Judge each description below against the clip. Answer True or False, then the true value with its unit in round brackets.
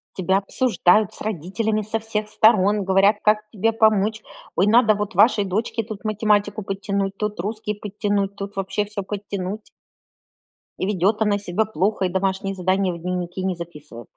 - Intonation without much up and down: True (2.1 semitones)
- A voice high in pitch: True (205 Hz)